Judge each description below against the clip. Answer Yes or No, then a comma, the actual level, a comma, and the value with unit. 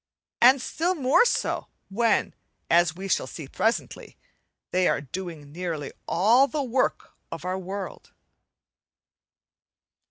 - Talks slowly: Yes, slow, 120 wpm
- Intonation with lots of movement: Yes, wide, 6.6 semitones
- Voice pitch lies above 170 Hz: Yes, high, 190 Hz